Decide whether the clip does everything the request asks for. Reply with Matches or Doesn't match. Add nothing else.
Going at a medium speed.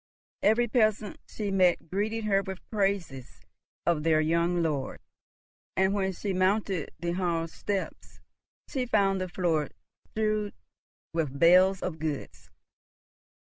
Doesn't match